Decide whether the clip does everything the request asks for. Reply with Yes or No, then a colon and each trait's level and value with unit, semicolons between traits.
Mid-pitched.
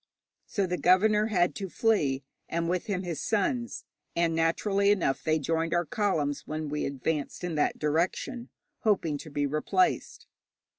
Yes: medium, 170 Hz